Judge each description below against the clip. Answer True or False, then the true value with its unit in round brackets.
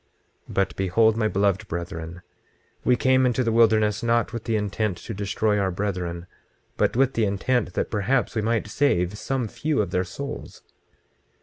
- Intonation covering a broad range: False (3.4 semitones)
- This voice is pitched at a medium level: False (105 Hz)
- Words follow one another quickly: False (175 wpm)